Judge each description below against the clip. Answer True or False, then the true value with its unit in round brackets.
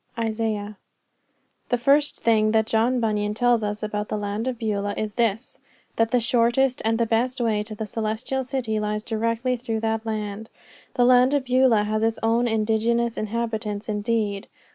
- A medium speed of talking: True (170 wpm)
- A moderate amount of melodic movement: False (1.8 semitones)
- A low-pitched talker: False (225 Hz)